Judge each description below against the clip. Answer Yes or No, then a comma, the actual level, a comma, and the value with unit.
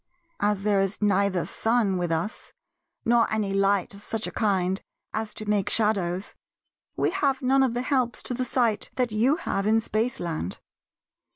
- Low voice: No, high, 210 Hz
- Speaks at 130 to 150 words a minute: No, average, 170 wpm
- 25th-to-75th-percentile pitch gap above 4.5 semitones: No, average, 3.4 semitones